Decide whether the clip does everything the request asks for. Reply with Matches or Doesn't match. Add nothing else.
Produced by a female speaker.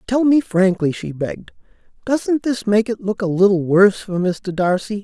Doesn't match